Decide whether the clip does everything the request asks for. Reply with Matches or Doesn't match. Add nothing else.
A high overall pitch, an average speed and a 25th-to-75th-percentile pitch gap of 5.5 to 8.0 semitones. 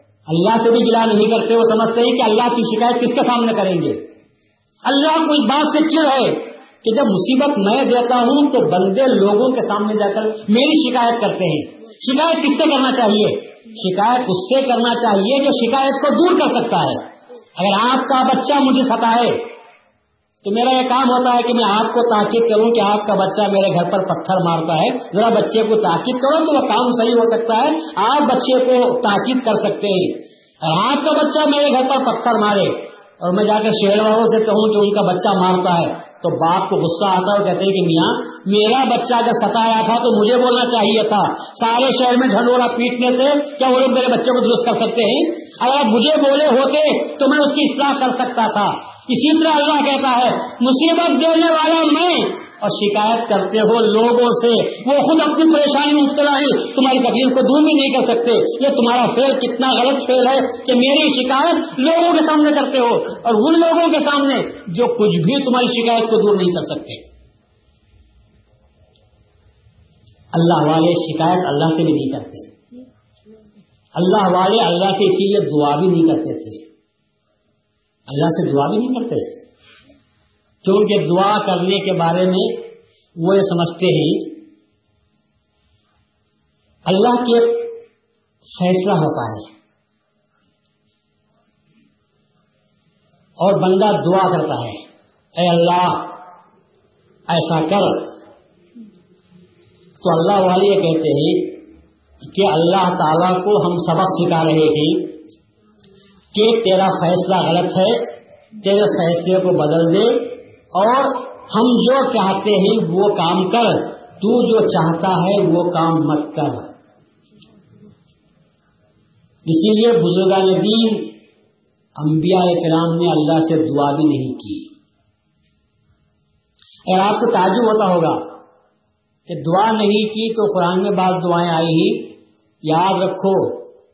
Matches